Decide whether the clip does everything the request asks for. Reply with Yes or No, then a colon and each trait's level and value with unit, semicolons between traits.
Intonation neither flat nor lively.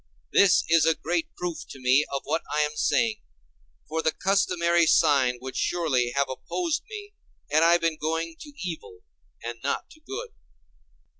Yes: average, 3.9 semitones